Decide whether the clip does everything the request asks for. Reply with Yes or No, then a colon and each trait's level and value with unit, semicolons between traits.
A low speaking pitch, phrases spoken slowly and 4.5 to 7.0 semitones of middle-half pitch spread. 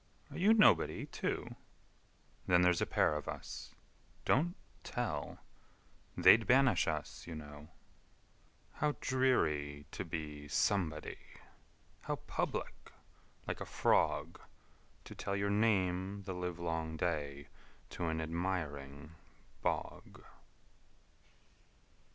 Yes: very low, 85 Hz; slow, 90 wpm; average, 4.9 semitones